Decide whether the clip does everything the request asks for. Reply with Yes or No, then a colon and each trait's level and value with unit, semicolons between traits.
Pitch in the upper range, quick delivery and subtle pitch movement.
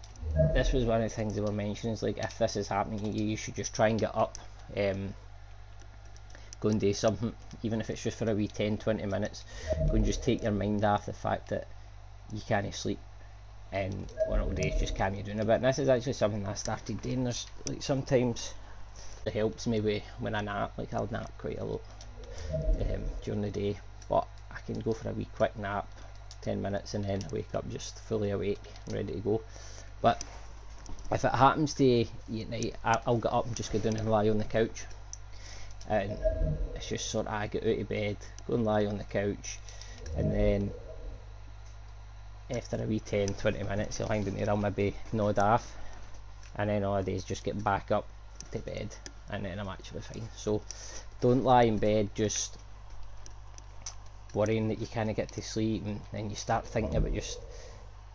No: low, 105 Hz; fast, 210 wpm; narrow, 1.6 semitones